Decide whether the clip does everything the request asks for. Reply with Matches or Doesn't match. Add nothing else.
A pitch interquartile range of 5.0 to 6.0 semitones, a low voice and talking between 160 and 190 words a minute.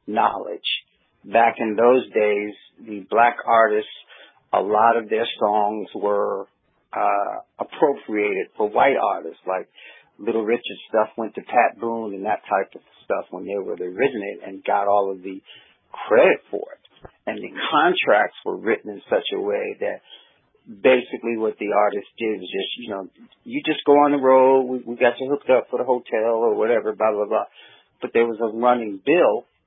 Matches